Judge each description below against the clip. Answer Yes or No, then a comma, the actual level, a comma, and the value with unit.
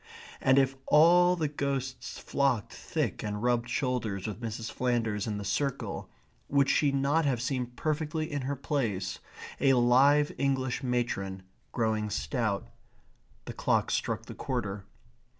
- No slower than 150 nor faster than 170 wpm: No, average, 140 wpm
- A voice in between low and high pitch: No, low, 125 Hz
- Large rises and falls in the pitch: No, average, 4.1 semitones